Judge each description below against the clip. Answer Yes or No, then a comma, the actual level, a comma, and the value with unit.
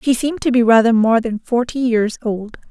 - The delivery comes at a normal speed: No, fast, 220 wpm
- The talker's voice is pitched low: No, high, 235 Hz